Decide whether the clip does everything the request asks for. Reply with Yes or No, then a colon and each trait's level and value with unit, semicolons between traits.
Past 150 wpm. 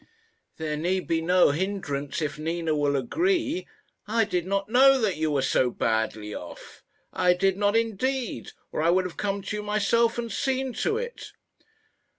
Yes: average, 170 wpm